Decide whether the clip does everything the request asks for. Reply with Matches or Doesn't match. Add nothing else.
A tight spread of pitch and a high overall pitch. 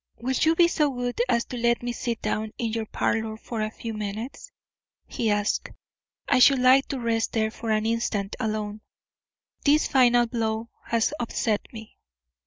Matches